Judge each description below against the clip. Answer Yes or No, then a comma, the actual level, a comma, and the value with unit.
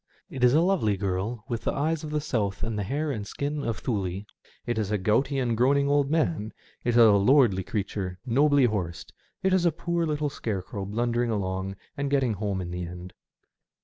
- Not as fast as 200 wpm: No, fast, 205 wpm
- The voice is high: No, low, 115 Hz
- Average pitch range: No, wide, 6.0 semitones